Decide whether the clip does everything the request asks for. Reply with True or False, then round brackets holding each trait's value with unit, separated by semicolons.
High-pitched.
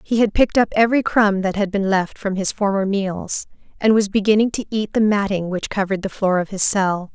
True (200 Hz)